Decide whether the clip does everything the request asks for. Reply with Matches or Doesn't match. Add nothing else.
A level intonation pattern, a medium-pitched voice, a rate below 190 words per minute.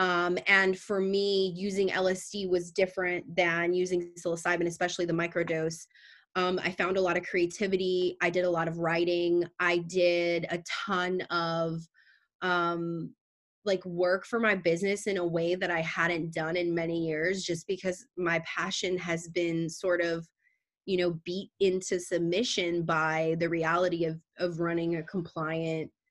Matches